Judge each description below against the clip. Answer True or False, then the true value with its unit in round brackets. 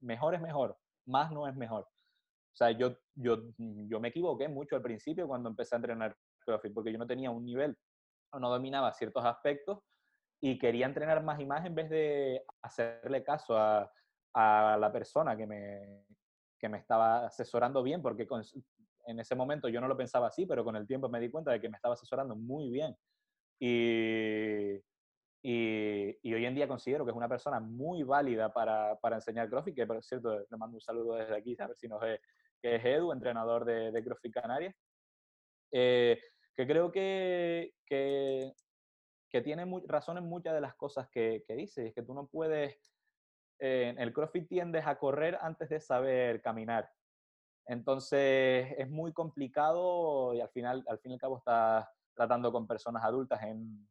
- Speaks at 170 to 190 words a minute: True (185 wpm)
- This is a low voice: True (125 Hz)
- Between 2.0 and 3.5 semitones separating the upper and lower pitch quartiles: False (4.2 semitones)